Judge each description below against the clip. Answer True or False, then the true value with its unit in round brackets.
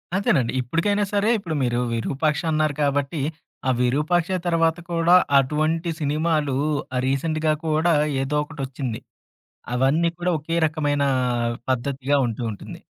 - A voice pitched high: False (150 Hz)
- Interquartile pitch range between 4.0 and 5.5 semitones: False (3.5 semitones)